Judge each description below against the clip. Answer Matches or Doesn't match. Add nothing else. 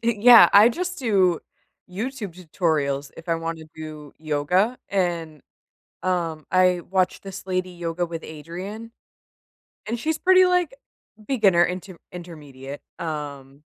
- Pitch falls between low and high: Matches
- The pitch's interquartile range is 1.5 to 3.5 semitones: Doesn't match